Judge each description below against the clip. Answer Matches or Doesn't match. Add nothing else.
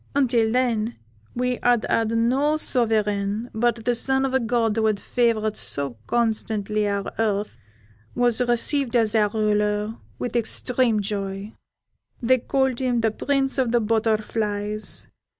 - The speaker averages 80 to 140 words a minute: Matches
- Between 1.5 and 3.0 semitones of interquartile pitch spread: Matches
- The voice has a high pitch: Matches